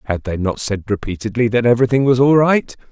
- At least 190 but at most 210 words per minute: Yes, fast, 205 wpm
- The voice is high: No, low, 115 Hz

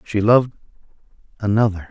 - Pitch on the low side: Yes, low, 105 Hz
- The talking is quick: No, slow, 95 wpm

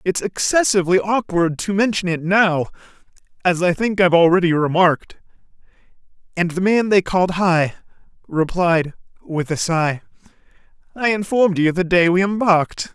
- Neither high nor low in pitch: Yes, medium, 180 Hz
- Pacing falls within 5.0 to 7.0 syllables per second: Yes, 5.1 syllables/s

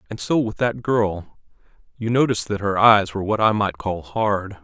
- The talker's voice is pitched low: Yes, low, 105 Hz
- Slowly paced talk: No, fast, 205 wpm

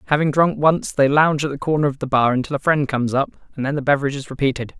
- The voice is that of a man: Yes, male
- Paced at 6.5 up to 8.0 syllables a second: Yes, 7.1 syllables/s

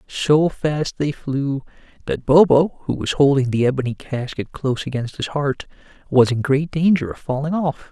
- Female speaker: No, male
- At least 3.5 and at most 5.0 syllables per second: Yes, 4.7 syllables/s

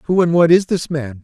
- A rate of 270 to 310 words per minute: Yes, fast, 290 wpm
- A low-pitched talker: No, medium, 160 Hz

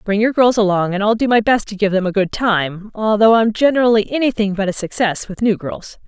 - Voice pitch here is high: Yes, high, 210 Hz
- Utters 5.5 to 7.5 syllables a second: Yes, 5.6 syllables/s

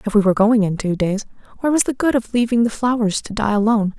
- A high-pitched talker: Yes, high, 220 Hz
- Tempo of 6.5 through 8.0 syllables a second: Yes, 6.8 syllables/s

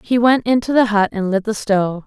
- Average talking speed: No, fast, 260 wpm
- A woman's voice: Yes, female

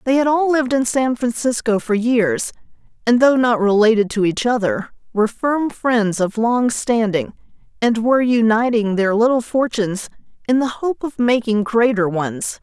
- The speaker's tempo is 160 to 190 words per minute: Yes, average, 165 wpm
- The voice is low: No, high, 230 Hz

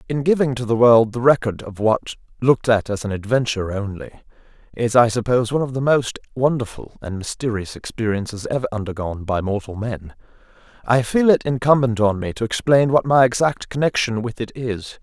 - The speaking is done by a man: Yes, male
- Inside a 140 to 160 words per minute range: No, average, 185 wpm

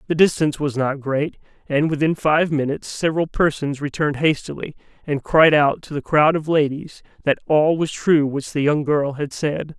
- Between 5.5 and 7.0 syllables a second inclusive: No, 5.1 syllables/s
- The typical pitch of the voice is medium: Yes, medium, 150 Hz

